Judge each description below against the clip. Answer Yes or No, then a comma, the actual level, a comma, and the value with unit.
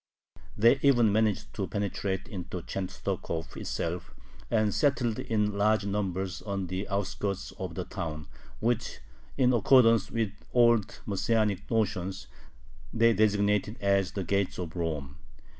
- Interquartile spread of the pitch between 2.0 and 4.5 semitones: Yes, average, 2.9 semitones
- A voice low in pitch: Yes, low, 100 Hz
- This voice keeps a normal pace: No, slow, 125 wpm